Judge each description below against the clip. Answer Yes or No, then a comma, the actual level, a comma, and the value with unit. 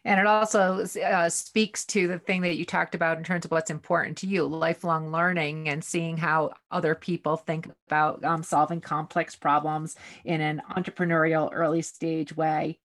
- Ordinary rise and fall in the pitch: No, narrow, 2.2 semitones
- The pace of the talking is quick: No, average, 175 wpm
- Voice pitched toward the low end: No, medium, 165 Hz